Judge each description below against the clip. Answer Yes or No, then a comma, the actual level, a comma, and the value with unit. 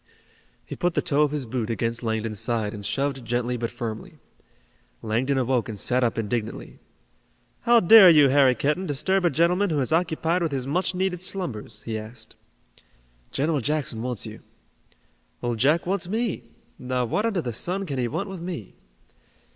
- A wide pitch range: Yes, wide, 6.8 semitones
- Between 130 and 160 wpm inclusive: No, average, 175 wpm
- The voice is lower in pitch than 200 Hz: Yes, low, 135 Hz